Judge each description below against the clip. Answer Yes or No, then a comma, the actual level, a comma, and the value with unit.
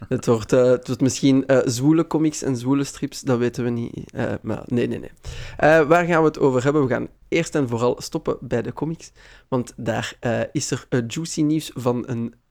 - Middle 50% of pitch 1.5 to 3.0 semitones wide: No, average, 3.7 semitones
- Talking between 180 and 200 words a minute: No, fast, 225 wpm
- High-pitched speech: No, low, 135 Hz